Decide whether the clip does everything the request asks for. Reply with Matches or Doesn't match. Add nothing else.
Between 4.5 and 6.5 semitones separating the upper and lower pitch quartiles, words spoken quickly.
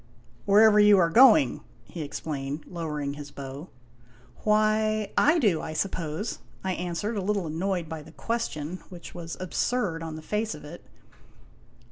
Doesn't match